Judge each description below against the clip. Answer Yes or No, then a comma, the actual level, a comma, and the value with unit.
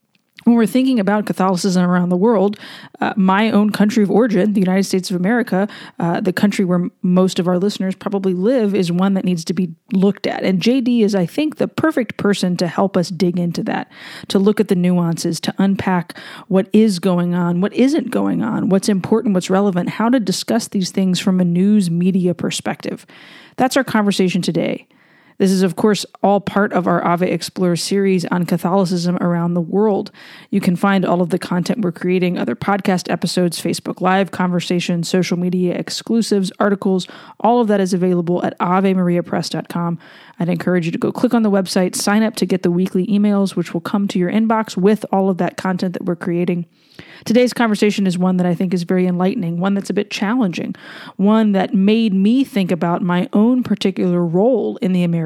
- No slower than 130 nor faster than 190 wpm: No, average, 200 wpm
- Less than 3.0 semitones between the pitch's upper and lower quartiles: Yes, narrow, 2.5 semitones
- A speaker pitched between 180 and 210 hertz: Yes, high, 190 Hz